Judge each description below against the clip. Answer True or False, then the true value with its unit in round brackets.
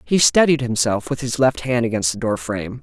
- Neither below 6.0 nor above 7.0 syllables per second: False (5.5 syllables/s)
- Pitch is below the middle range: True (125 Hz)